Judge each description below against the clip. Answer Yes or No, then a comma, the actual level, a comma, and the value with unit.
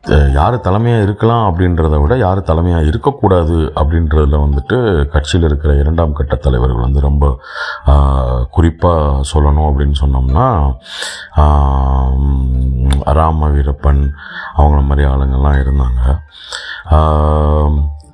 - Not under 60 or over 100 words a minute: Yes, average, 90 wpm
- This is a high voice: No, very low, 75 Hz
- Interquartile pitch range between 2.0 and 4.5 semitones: Yes, average, 2.7 semitones